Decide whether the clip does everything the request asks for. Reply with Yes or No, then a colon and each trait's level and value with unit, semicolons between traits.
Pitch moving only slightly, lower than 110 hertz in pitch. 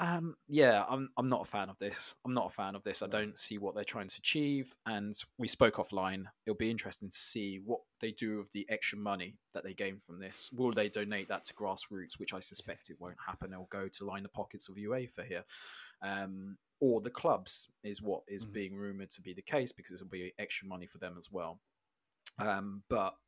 Yes: narrow, 2.3 semitones; low, 100 Hz